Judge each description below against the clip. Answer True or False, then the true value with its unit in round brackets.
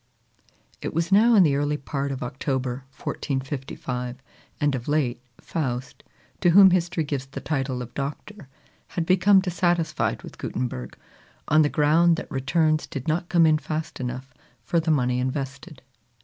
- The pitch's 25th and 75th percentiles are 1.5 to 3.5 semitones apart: False (4.1 semitones)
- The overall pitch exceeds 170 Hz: False (145 Hz)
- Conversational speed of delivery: True (155 wpm)